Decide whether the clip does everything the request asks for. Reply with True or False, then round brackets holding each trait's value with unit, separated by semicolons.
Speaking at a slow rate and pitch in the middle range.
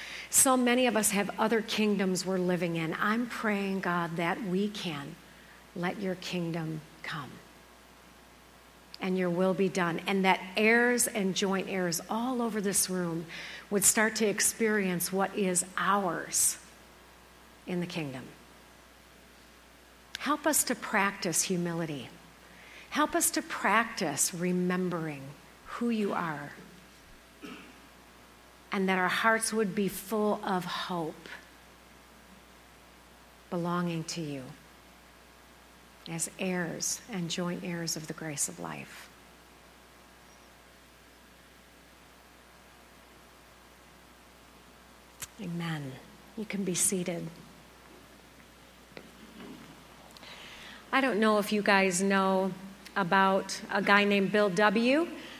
True (105 wpm; 175 Hz)